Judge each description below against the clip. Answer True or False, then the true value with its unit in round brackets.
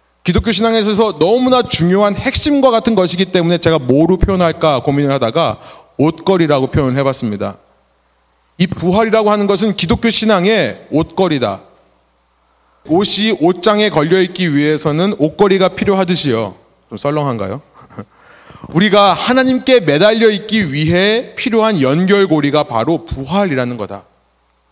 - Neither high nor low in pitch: True (175 Hz)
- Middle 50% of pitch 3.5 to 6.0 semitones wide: False (7.2 semitones)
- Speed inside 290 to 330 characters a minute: True (320 characters per minute)